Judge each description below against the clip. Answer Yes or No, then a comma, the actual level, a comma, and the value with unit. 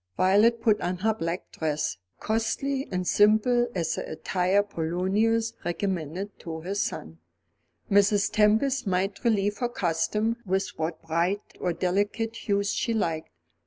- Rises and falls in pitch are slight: No, average, 3.8 semitones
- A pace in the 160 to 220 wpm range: No, slow, 135 wpm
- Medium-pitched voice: No, high, 200 Hz